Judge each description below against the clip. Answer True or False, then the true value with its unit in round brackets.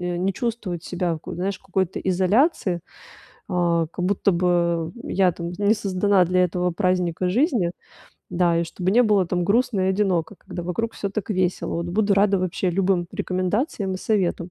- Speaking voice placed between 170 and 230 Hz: True (185 Hz)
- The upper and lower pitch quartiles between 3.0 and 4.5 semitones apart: False (2.4 semitones)